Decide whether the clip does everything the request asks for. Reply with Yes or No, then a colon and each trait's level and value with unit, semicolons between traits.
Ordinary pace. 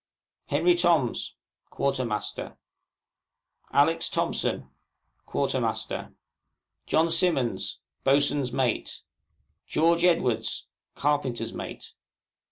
No: slow, 65 wpm